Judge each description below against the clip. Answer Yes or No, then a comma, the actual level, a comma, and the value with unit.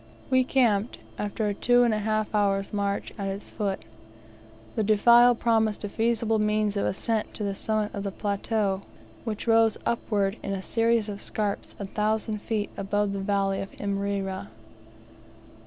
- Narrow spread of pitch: Yes, narrow, 1.9 semitones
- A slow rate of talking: No, average, 165 wpm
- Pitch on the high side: Yes, high, 210 Hz